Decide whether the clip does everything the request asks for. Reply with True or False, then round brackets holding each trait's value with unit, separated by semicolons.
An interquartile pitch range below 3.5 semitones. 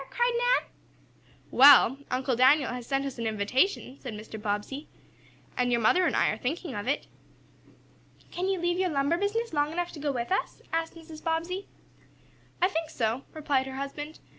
False (5.5 semitones)